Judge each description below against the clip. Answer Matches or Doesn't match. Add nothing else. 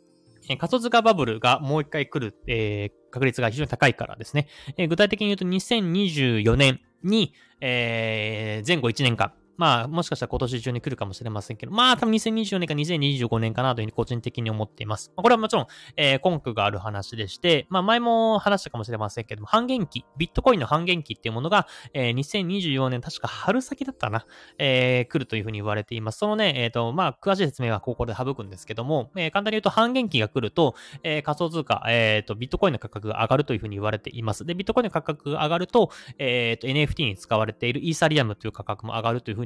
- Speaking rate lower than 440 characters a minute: Doesn't match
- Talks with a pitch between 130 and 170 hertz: Matches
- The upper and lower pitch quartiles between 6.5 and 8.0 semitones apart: Matches